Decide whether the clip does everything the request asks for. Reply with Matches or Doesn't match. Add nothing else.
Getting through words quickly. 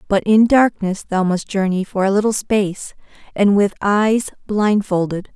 Doesn't match